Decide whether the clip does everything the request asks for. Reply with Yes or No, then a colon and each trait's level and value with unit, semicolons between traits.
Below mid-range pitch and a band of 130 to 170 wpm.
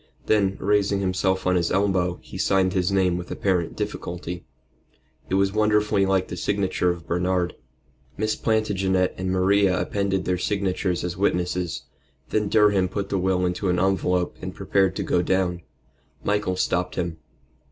Yes: very low, 95 Hz; average, 155 wpm